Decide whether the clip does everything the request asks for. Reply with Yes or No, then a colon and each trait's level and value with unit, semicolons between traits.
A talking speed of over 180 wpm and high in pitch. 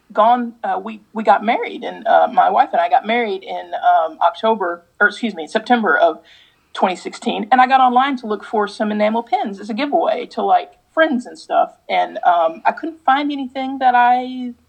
Yes: average, 200 wpm; high, 245 Hz